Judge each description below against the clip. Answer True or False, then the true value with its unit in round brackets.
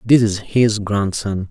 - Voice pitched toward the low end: True (105 Hz)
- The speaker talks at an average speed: True (160 wpm)